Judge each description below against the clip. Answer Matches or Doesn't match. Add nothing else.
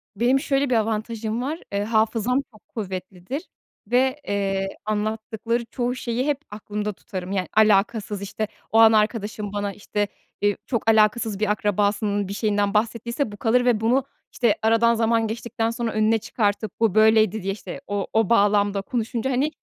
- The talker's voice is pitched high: Matches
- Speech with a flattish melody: Matches